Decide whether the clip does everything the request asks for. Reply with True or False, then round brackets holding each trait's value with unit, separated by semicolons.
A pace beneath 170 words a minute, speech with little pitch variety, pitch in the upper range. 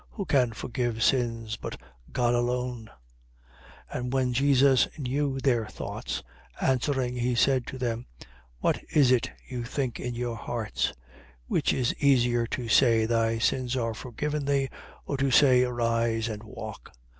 False (155 wpm; 2.3 semitones; 125 Hz)